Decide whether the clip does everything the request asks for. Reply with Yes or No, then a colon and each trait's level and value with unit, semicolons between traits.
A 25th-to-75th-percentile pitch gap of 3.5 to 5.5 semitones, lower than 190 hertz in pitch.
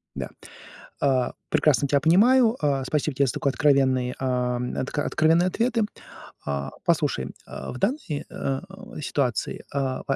Yes: average, 4.0 semitones; medium, 140 Hz